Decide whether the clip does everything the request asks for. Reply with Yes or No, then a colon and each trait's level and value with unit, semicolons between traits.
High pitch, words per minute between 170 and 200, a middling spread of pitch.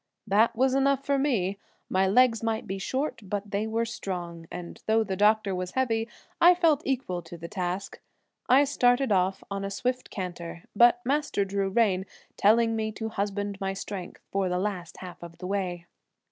Yes: high, 205 Hz; average, 185 wpm; average, 4.2 semitones